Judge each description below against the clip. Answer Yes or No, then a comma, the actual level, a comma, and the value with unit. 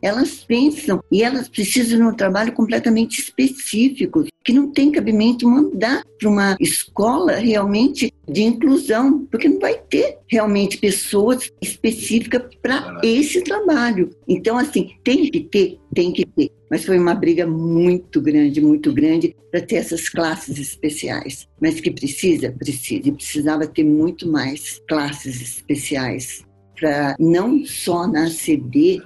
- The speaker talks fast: No, average, 140 wpm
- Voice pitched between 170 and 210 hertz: No, high, 220 Hz